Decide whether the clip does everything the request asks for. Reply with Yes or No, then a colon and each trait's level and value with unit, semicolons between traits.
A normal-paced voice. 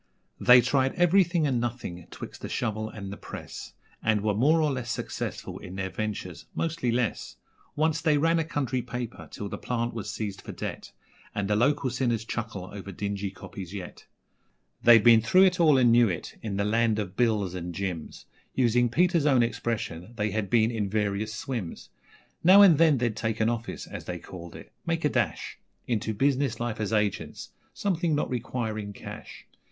Yes: average, 185 wpm